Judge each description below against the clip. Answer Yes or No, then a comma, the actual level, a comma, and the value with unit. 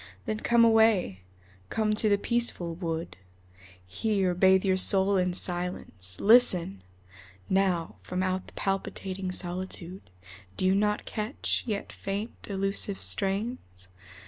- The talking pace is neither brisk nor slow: No, slow, 120 wpm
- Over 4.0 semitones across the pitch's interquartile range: No, average, 2.8 semitones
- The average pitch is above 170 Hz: Yes, high, 190 Hz